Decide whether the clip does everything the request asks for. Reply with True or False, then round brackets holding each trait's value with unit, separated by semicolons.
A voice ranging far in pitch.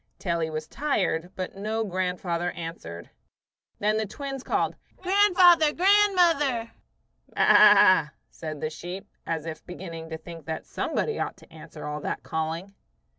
True (8.8 semitones)